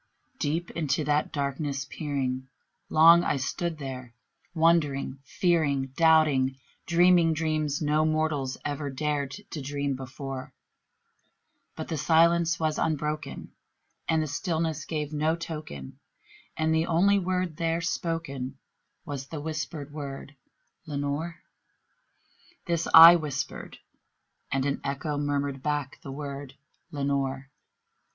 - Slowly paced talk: Yes, slow, 115 wpm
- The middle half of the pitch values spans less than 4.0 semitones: Yes, average, 2.7 semitones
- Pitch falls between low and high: Yes, medium, 150 Hz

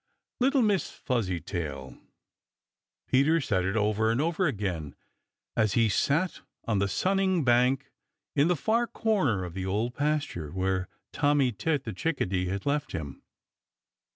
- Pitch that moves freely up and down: Yes, wide, 8.3 semitones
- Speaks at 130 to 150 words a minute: Yes, average, 140 wpm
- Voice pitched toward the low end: Yes, low, 120 Hz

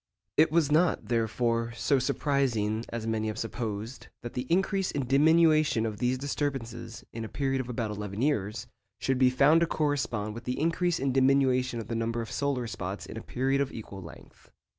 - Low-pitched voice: Yes, low, 125 Hz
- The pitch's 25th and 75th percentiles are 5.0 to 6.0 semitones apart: No, average, 3.9 semitones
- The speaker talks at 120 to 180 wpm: No, average, 190 wpm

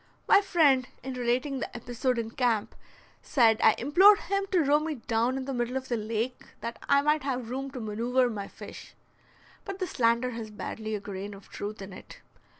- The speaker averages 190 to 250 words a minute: Yes, average, 200 wpm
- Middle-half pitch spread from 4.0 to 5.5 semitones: No, average, 3.6 semitones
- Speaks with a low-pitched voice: No, very high, 250 Hz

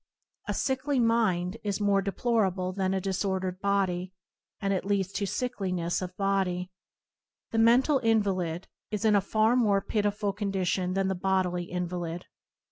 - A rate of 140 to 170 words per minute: Yes, average, 145 wpm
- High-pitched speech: Yes, high, 195 Hz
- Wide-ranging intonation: No, narrow, 2.5 semitones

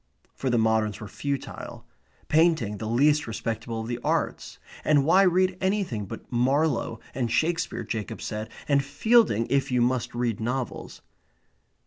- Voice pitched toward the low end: Yes, low, 125 Hz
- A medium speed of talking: Yes, average, 145 wpm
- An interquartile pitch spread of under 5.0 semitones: No, wide, 5.4 semitones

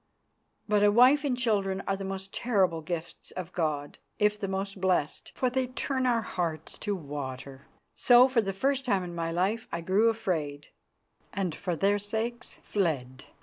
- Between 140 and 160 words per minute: No, average, 175 wpm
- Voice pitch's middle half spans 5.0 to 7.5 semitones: Yes, wide, 5.4 semitones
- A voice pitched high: Yes, high, 195 Hz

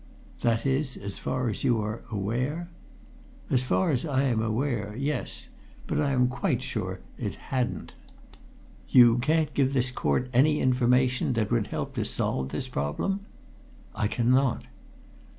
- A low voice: Yes, low, 125 Hz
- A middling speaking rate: Yes, average, 150 wpm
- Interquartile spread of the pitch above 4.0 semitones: No, average, 3.0 semitones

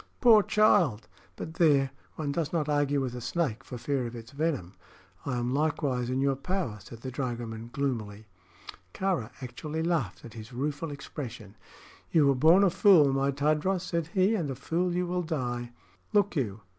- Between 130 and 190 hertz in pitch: Yes, medium, 140 Hz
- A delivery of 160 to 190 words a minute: Yes, average, 180 wpm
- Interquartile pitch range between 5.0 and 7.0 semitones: Yes, average, 5.3 semitones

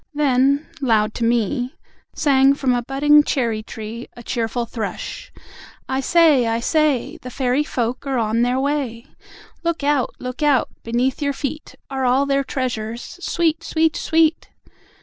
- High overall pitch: Yes, very high, 265 Hz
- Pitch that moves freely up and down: No, average, 3.6 semitones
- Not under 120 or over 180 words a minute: Yes, average, 150 wpm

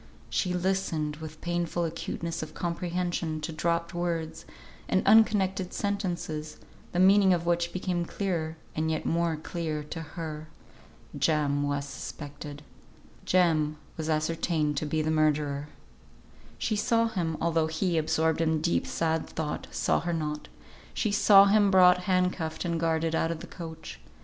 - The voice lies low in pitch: No, medium, 165 Hz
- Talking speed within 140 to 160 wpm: Yes, average, 150 wpm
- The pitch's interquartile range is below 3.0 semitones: Yes, narrow, 2.4 semitones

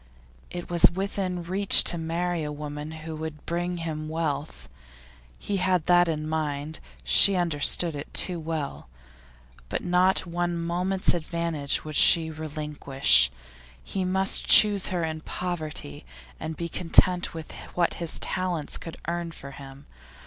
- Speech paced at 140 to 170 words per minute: Yes, average, 150 wpm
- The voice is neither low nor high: Yes, medium, 165 Hz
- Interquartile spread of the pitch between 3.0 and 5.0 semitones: No, narrow, 2.5 semitones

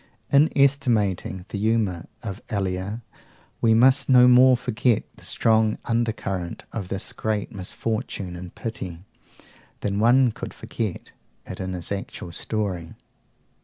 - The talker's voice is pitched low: Yes, low, 110 Hz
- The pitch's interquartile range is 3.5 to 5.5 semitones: Yes, average, 4.0 semitones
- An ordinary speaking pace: No, slow, 130 wpm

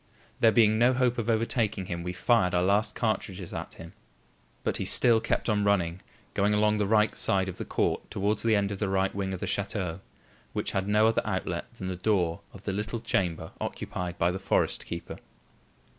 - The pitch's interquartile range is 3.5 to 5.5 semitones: No, average, 2.8 semitones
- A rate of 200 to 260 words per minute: Yes, fast, 205 wpm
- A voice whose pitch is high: No, low, 100 Hz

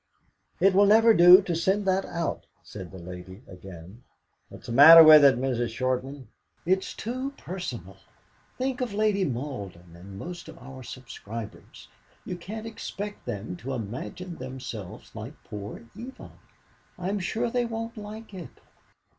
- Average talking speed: Yes, average, 150 wpm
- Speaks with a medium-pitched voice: Yes, medium, 150 Hz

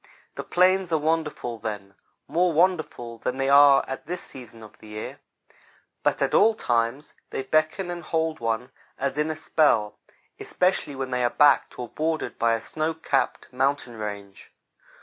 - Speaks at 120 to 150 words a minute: No, average, 170 wpm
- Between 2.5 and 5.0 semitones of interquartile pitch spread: No, wide, 5.4 semitones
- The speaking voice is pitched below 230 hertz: Yes, medium, 140 Hz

